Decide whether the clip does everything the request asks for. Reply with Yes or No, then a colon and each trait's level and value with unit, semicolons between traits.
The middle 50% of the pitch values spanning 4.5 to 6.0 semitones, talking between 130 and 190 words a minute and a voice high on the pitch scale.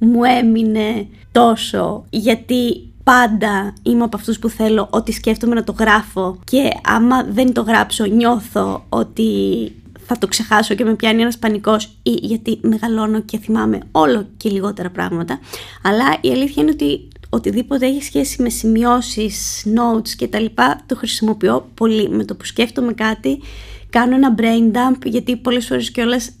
No: average, 2.8 semitones; average, 155 wpm; high, 220 Hz